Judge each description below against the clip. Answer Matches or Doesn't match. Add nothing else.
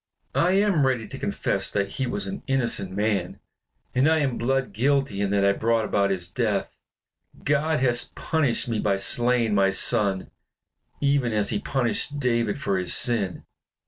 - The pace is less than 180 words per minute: Matches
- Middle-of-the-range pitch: Doesn't match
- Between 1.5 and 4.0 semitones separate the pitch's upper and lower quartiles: Doesn't match